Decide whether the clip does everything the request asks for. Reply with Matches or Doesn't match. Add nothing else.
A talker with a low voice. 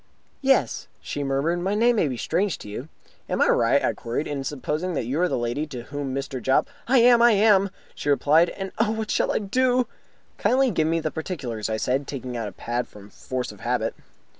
Doesn't match